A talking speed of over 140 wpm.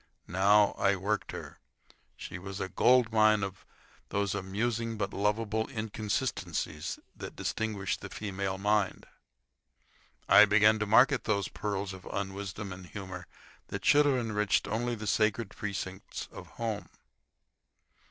No: slow, 135 wpm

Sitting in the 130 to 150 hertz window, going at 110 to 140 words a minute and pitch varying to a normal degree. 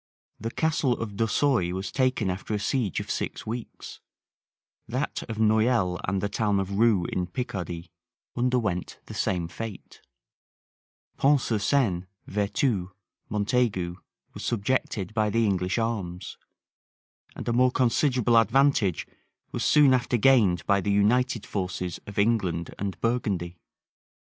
No: low, 105 Hz; slow, 135 wpm; average, 4.5 semitones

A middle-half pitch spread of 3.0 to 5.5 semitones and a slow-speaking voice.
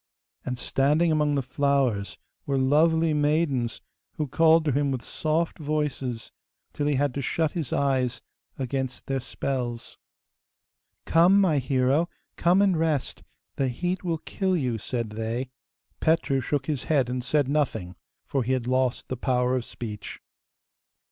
No: average, 3.6 semitones; average, 150 wpm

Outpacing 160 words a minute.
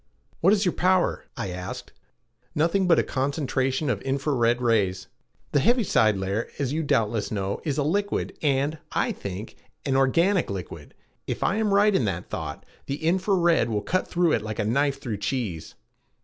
Yes: average, 180 wpm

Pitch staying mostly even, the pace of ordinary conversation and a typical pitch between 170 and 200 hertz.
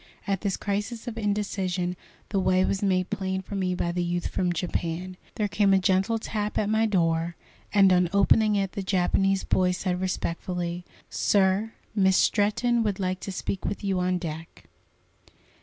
Yes: narrow, 2.2 semitones; average, 175 wpm; high, 190 Hz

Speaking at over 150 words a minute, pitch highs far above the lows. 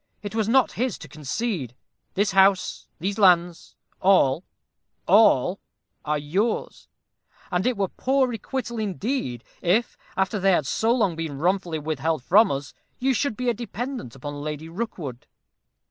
No: average, 145 wpm; wide, 6.5 semitones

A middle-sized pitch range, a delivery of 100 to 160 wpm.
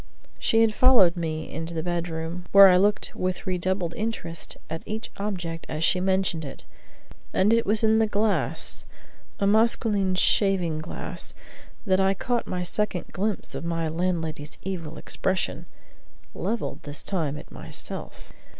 Yes: average, 3.8 semitones; average, 150 wpm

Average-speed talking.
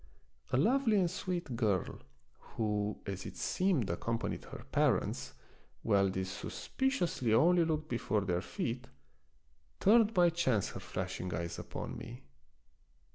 No: slow, 130 wpm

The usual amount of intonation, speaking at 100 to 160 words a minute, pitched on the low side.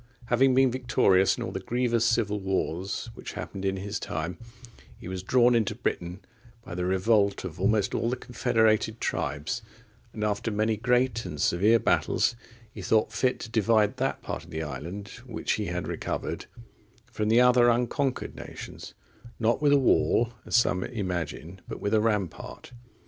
No: average, 4.1 semitones; average, 170 wpm; low, 110 Hz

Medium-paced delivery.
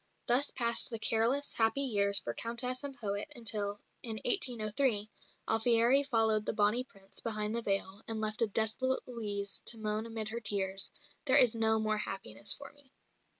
Yes: average, 170 wpm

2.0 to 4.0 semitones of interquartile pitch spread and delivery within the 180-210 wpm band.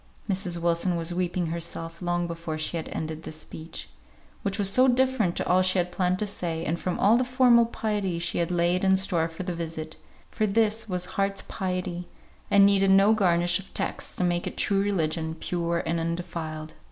Yes: average, 2.8 semitones; average, 200 wpm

